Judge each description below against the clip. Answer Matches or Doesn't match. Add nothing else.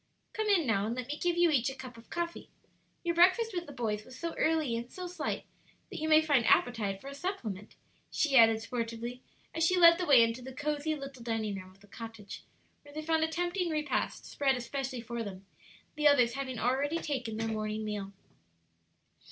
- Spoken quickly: Matches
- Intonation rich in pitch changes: Matches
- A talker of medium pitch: Doesn't match